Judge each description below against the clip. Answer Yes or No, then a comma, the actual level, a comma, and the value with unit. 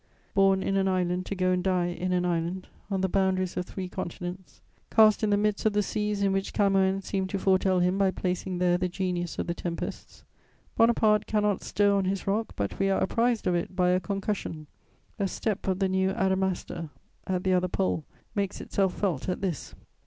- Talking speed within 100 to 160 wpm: No, fast, 205 wpm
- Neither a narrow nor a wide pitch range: No, narrow, 1.6 semitones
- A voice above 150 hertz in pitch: Yes, high, 190 Hz